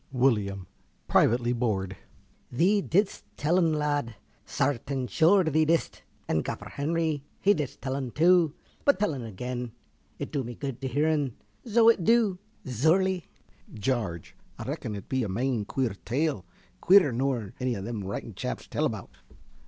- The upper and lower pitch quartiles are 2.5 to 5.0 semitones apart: No, wide, 5.6 semitones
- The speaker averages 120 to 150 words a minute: No, average, 160 wpm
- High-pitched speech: No, low, 135 Hz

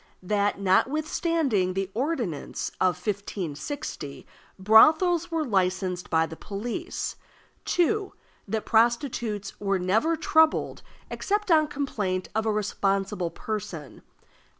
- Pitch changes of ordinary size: No, wide, 8.3 semitones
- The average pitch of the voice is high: Yes, high, 210 Hz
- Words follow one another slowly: Yes, slow, 105 wpm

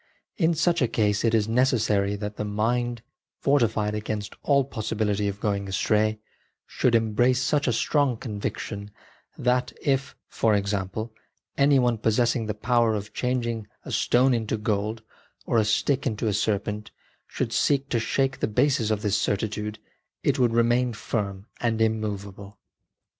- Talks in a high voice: No, low, 110 Hz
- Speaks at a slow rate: No, average, 155 wpm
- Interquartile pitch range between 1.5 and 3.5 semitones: Yes, average, 2.9 semitones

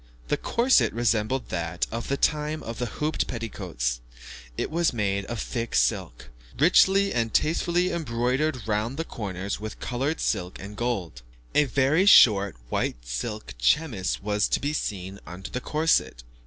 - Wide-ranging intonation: Yes, wide, 7.3 semitones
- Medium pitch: No, low, 115 Hz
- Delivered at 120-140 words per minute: No, average, 155 wpm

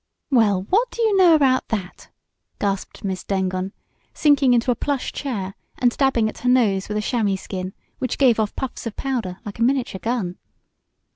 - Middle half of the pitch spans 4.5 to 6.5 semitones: Yes, average, 5.3 semitones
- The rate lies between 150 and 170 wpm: No, average, 185 wpm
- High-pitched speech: Yes, high, 230 Hz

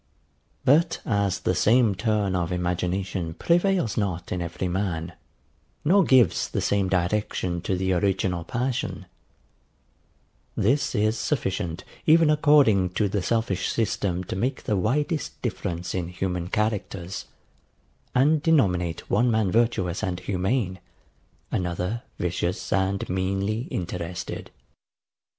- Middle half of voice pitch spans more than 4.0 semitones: Yes, average, 4.5 semitones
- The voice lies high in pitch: No, very low, 95 Hz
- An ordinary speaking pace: No, slow, 120 wpm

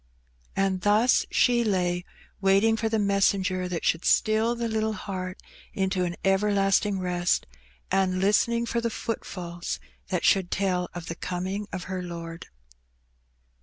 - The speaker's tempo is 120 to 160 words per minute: Yes, average, 140 wpm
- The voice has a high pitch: Yes, high, 195 Hz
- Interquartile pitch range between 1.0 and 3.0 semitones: Yes, average, 2.7 semitones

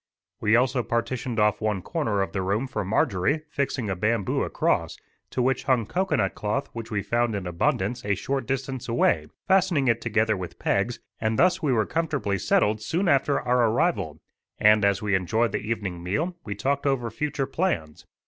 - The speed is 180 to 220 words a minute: Yes, average, 185 wpm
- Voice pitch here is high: No, low, 115 Hz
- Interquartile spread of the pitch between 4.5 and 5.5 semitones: Yes, average, 4.8 semitones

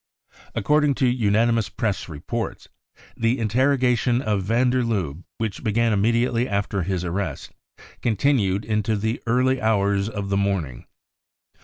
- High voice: No, low, 110 Hz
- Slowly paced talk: Yes, slow, 130 wpm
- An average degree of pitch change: Yes, average, 3.5 semitones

